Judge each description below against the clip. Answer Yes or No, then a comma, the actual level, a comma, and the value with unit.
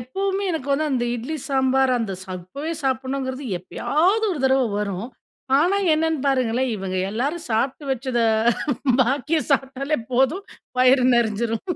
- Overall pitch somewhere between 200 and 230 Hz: No, very high, 265 Hz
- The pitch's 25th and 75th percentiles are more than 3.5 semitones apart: Yes, average, 4.0 semitones